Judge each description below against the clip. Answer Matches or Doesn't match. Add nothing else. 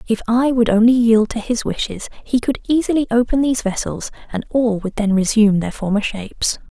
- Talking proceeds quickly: Doesn't match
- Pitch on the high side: Matches